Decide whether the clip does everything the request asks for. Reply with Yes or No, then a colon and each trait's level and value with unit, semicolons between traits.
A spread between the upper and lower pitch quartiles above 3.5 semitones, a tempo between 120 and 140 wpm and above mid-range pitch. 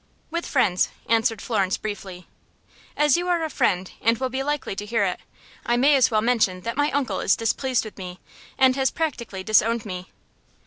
No: average, 5.2 semitones; average, 190 wpm; high, 230 Hz